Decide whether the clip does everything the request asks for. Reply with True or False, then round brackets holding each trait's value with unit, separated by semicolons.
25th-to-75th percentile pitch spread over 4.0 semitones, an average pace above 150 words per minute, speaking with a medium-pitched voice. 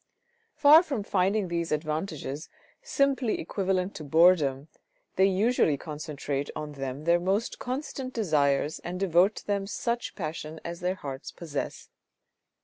False (5.1 semitones; 140 wpm; 175 Hz)